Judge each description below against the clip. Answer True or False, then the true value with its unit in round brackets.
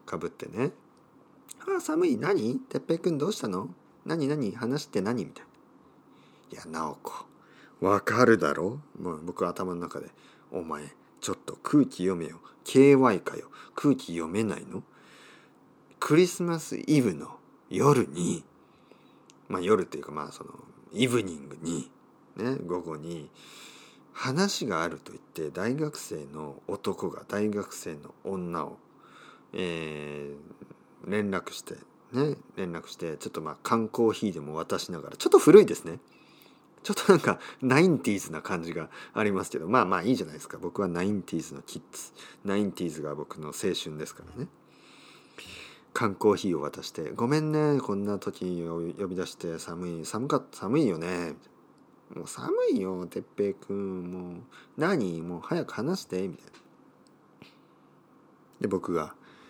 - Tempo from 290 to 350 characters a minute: False (280 characters per minute)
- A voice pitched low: True (95 Hz)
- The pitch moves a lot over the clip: True (7.8 semitones)